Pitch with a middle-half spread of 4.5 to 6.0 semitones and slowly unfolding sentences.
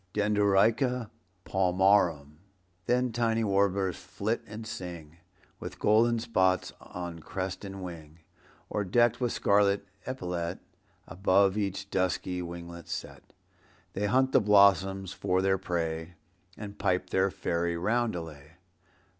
No: average, 3.1 semitones; slow, 115 wpm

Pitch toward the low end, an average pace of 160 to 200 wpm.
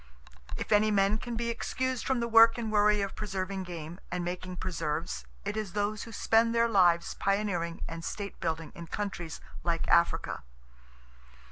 No: high, 200 Hz; average, 165 wpm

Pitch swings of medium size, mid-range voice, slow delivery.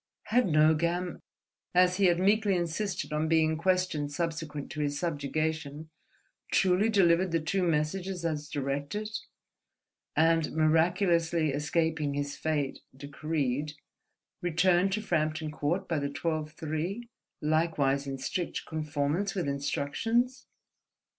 Yes: average, 3.2 semitones; medium, 160 Hz; slow, 115 wpm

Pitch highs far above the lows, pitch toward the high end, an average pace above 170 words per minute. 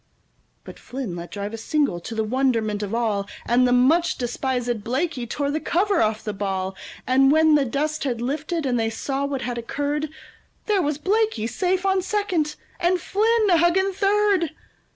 Yes: wide, 6.9 semitones; very high, 275 Hz; average, 180 wpm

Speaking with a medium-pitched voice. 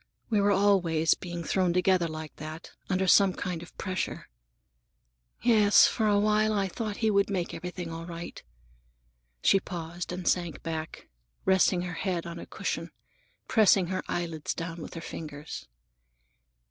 Yes: medium, 180 Hz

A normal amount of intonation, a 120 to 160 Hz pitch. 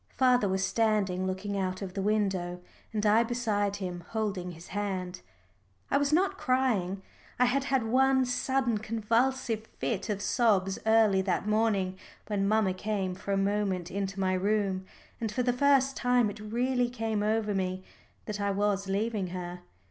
No: average, 3.4 semitones; high, 210 Hz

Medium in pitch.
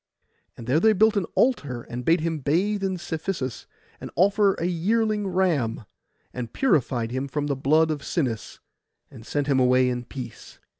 Yes: medium, 155 Hz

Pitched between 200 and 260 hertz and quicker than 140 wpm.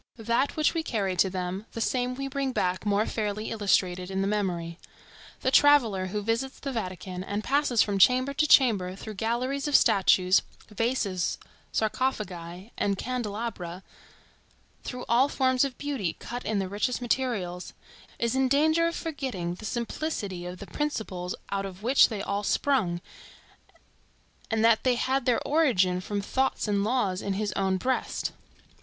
Yes: high, 215 Hz; average, 160 wpm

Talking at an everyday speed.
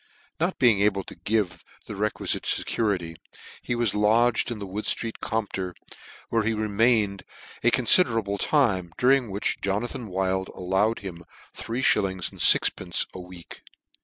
Yes: average, 150 wpm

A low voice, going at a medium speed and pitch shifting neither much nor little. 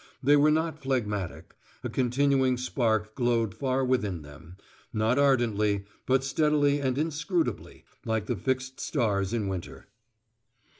No: low, 125 Hz; slow, 130 wpm; average, 4.7 semitones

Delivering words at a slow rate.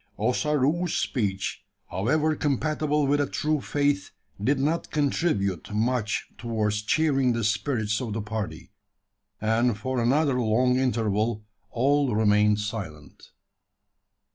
Yes: slow, 115 wpm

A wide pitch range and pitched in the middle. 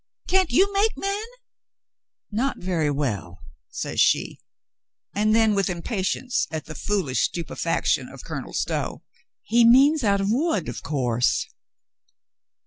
No: wide, 9.0 semitones; high, 205 Hz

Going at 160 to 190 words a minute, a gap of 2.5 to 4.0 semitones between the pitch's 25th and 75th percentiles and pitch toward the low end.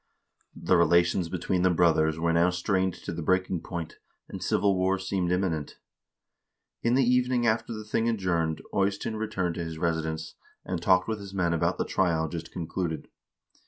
Yes: average, 170 wpm; average, 2.8 semitones; very low, 90 Hz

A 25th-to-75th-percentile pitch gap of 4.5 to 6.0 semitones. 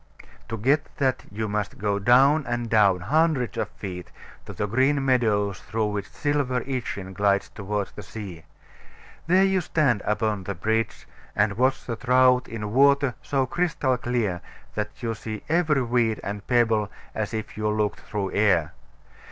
No: average, 4.1 semitones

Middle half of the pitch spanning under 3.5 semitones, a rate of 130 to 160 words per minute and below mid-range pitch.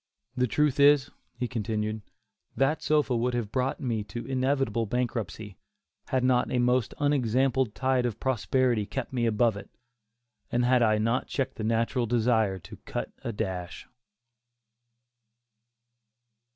Yes: average, 2.8 semitones; average, 140 wpm; low, 120 Hz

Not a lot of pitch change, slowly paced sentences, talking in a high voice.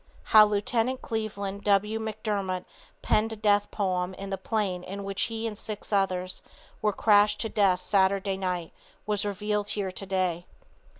No: narrow, 1.9 semitones; average, 155 wpm; high, 200 Hz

